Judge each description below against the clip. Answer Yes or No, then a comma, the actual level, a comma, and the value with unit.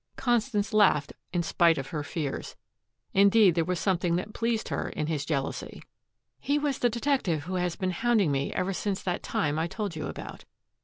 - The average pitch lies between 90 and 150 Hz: No, medium, 180 Hz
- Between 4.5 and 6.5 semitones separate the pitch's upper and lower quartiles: Yes, average, 5.1 semitones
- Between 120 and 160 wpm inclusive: No, average, 190 wpm